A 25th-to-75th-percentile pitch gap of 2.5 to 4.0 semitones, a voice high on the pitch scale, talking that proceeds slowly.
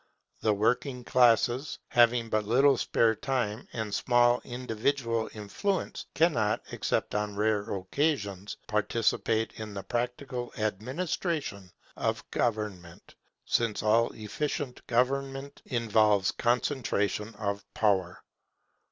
No: average, 3.2 semitones; low, 115 Hz; slow, 100 wpm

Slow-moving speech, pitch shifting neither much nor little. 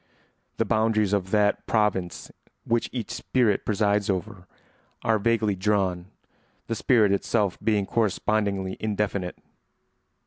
No: slow, 110 wpm; narrow, 2.2 semitones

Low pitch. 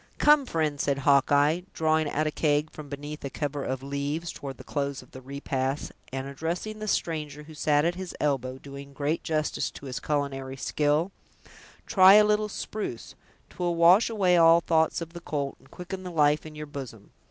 No: medium, 150 Hz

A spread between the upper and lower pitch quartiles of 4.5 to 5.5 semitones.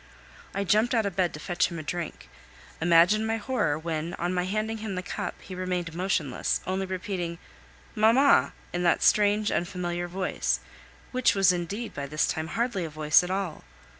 No: average, 3.4 semitones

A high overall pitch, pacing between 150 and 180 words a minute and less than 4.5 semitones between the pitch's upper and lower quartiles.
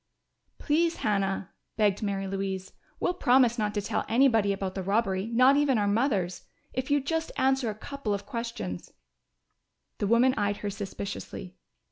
No: high, 215 Hz; average, 160 wpm; average, 4.8 semitones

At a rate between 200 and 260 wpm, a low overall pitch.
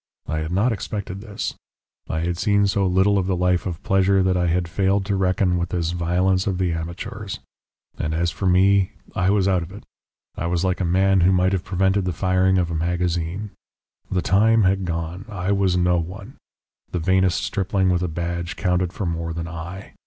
Yes: fast, 205 wpm; very low, 90 Hz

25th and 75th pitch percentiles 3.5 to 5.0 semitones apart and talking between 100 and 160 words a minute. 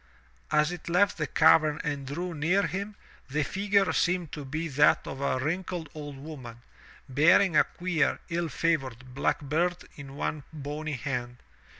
Yes: average, 3.9 semitones; average, 155 wpm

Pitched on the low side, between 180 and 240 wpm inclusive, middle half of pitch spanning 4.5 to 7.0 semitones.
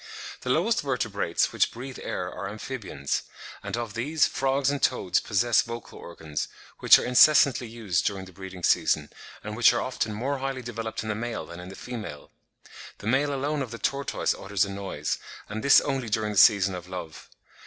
Yes: low, 110 Hz; average, 190 wpm; average, 5.1 semitones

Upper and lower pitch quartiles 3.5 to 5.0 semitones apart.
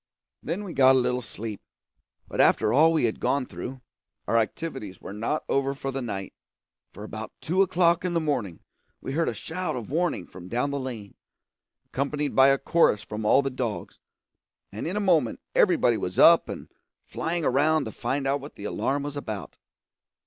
No: wide, 5.5 semitones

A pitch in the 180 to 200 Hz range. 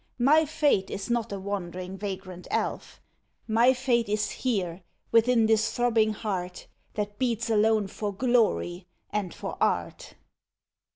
No: high, 215 Hz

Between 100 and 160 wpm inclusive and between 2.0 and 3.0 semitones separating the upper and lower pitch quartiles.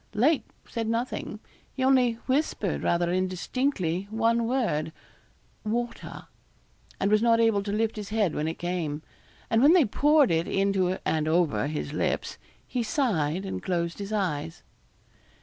No: average, 150 wpm; wide, 5.5 semitones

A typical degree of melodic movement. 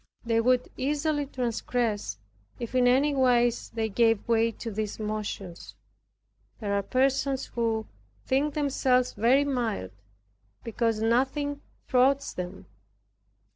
Yes: average, 3.1 semitones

